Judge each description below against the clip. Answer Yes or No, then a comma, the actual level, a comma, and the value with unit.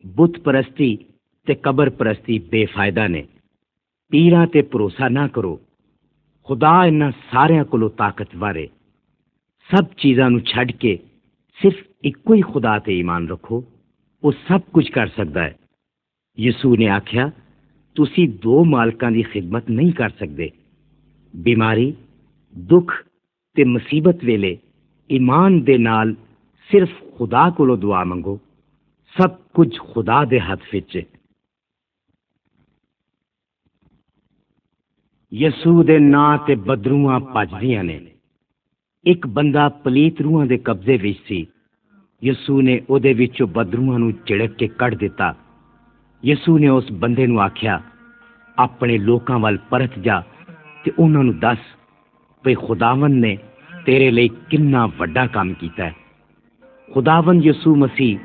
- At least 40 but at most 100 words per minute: No, average, 125 wpm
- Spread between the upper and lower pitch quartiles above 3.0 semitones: Yes, average, 5.2 semitones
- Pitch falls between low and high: No, low, 125 Hz